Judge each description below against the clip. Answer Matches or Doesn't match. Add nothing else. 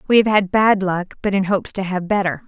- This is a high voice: Matches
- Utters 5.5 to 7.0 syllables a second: Matches